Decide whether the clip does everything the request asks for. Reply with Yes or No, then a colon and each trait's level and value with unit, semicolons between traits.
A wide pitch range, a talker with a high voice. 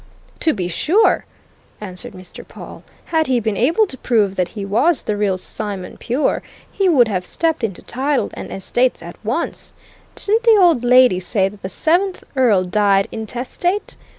Yes: wide, 8.2 semitones; high, 235 Hz